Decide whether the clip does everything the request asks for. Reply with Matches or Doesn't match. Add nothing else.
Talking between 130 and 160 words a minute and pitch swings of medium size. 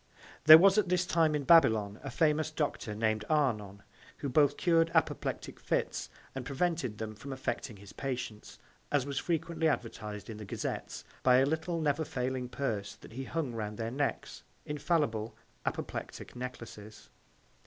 Doesn't match